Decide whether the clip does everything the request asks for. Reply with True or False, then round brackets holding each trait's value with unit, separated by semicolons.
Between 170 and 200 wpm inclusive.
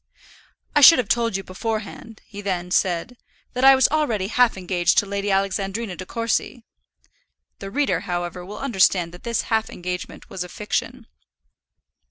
False (160 wpm)